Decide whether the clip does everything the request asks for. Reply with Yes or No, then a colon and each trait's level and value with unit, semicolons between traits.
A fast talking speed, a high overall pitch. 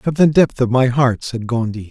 No: fast, 250 wpm; low, 125 Hz